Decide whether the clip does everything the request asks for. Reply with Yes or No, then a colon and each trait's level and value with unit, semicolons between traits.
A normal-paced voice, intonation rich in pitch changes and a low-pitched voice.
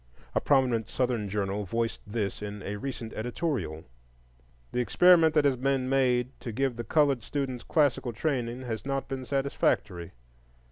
No: average, 150 wpm; average, 3.7 semitones; low, 125 Hz